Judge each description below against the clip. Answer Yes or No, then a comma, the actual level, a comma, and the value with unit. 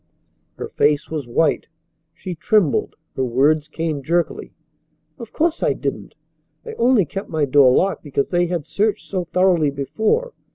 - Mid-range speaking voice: Yes, medium, 165 Hz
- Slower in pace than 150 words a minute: No, average, 155 wpm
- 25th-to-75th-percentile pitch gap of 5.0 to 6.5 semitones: Yes, wide, 5.4 semitones